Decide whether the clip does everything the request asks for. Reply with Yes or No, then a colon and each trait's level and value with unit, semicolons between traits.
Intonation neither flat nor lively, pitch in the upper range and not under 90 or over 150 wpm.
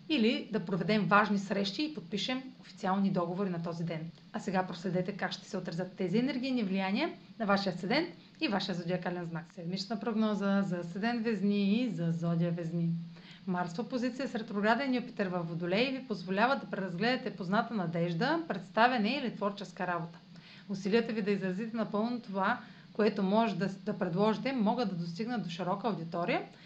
No: average, 4.0 semitones; high, 200 Hz; average, 160 wpm